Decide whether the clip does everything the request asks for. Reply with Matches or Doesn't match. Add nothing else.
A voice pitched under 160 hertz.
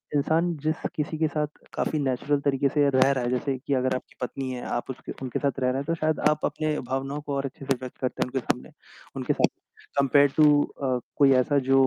Matches